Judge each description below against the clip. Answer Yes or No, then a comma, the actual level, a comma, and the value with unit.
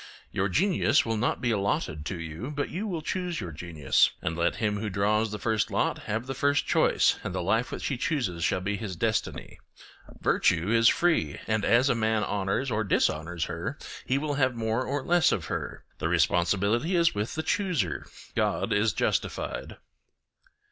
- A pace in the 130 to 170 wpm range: No, average, 180 wpm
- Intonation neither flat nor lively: No, wide, 6.4 semitones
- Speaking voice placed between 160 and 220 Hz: No, low, 110 Hz